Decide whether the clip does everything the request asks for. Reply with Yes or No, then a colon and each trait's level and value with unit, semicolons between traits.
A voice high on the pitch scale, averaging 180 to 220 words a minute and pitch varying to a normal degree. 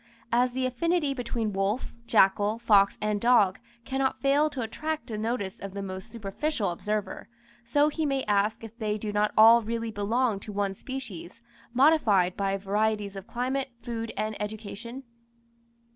No: high, 220 Hz; average, 160 wpm; average, 3.8 semitones